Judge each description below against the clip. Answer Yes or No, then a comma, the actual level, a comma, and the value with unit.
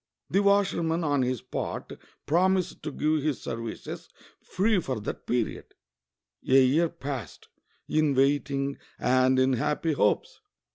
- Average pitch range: Yes, average, 4.2 semitones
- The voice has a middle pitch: Yes, medium, 145 Hz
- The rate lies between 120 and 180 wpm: Yes, slow, 135 wpm